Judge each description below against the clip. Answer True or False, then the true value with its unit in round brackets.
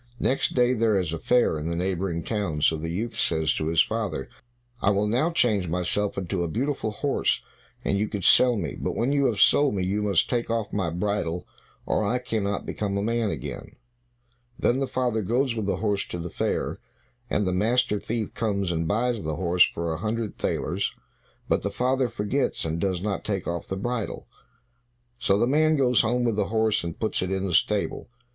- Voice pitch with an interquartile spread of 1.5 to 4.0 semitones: False (4.6 semitones)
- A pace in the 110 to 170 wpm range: False (205 wpm)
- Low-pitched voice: True (105 Hz)